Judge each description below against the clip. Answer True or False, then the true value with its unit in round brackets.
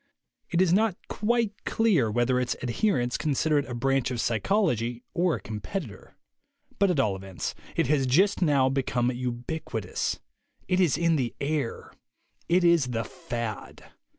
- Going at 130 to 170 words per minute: True (155 wpm)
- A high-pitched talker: False (135 Hz)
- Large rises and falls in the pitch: True (6.4 semitones)